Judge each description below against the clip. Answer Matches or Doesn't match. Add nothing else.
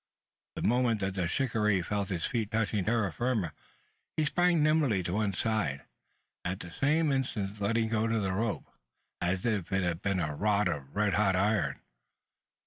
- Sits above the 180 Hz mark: Doesn't match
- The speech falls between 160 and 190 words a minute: Matches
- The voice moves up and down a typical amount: Matches